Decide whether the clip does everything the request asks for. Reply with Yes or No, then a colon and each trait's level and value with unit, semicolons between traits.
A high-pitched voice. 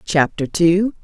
No: medium, 175 Hz